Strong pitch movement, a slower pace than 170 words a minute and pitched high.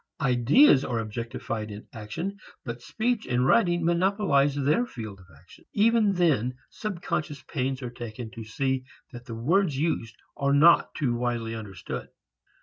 No: wide, 6.8 semitones; average, 145 wpm; low, 130 Hz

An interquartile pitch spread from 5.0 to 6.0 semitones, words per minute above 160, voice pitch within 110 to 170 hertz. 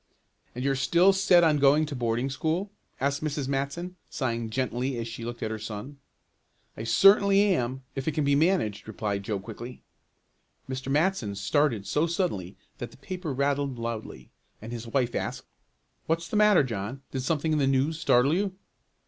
Yes: average, 5.3 semitones; average, 175 wpm; low, 135 Hz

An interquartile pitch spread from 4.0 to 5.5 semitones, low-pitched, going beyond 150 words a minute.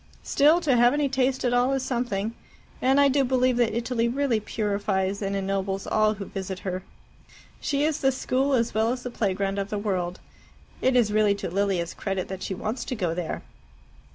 No: average, 4.6 semitones; high, 220 Hz; average, 200 wpm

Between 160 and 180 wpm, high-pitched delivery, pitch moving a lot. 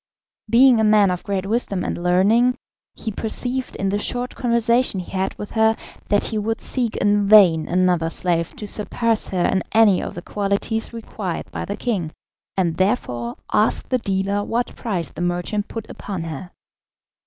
No: average, 175 wpm; high, 205 Hz; average, 3.6 semitones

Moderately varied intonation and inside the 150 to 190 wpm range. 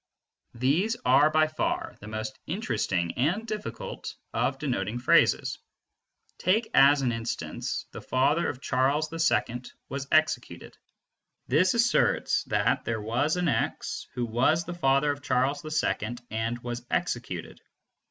No: average, 4.4 semitones; slow, 135 wpm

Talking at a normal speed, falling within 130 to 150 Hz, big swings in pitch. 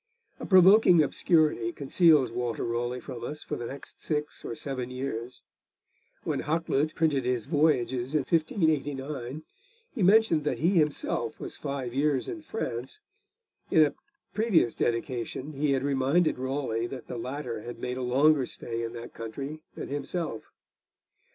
No: average, 150 wpm; medium, 140 Hz; average, 4.1 semitones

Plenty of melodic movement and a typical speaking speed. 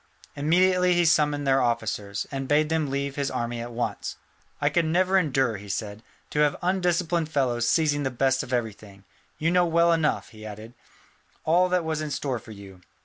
Yes: wide, 5.7 semitones; average, 190 wpm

